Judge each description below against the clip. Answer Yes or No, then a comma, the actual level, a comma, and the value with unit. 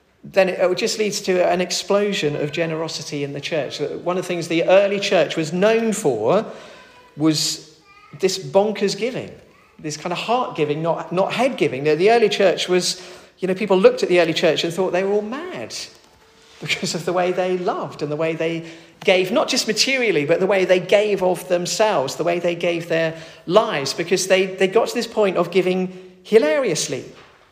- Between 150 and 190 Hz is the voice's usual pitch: Yes, medium, 185 Hz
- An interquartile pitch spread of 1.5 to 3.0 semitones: No, average, 3.6 semitones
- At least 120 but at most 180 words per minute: No, average, 195 wpm